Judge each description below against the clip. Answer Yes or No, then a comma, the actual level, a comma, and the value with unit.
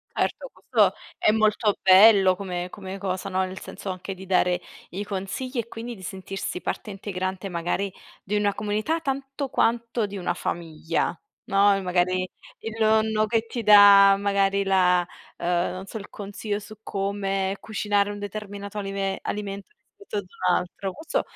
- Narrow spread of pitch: Yes, narrow, 2.1 semitones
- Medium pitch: No, high, 200 Hz